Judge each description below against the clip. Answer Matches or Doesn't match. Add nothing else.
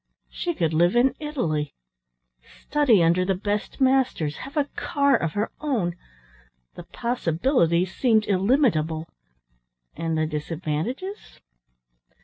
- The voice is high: Matches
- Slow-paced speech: Matches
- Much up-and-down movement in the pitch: Matches